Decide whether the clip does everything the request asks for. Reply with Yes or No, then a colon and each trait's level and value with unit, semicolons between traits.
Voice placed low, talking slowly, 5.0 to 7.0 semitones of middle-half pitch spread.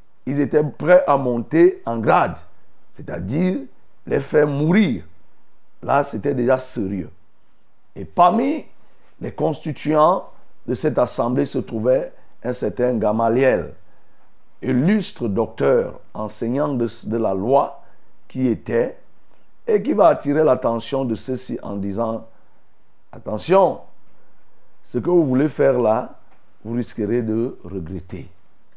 Yes: low, 130 Hz; slow, 115 wpm; wide, 5.4 semitones